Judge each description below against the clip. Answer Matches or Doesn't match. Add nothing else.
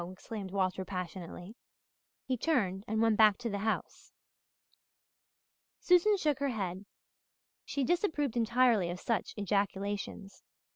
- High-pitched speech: Matches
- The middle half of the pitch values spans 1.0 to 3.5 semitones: Doesn't match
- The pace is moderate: Doesn't match